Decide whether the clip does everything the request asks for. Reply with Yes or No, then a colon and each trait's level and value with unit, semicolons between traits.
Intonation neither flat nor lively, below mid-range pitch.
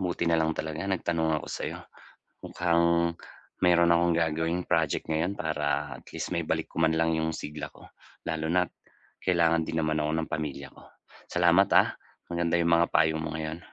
No: narrow, 1.3 semitones; very low, 80 Hz